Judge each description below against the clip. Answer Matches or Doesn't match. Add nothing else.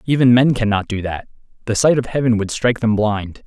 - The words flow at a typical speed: Doesn't match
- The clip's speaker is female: Doesn't match